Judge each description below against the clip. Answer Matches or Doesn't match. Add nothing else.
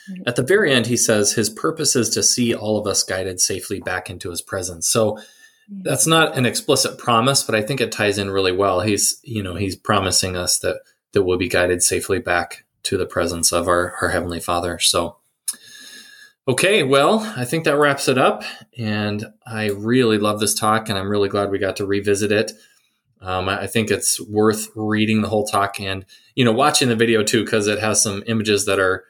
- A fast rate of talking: Matches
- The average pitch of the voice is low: Matches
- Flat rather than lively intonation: Doesn't match